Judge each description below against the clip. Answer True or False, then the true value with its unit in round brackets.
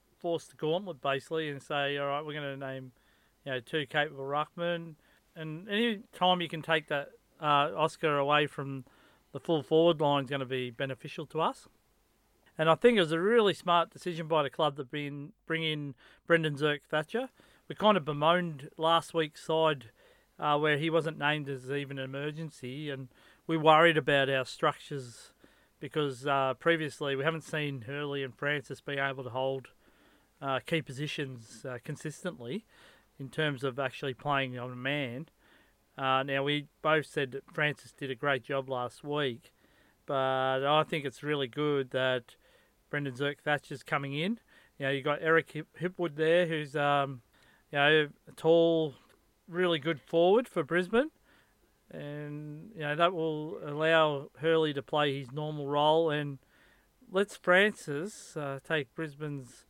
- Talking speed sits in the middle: True (170 wpm)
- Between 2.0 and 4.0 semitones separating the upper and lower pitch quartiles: True (2.8 semitones)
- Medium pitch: True (150 Hz)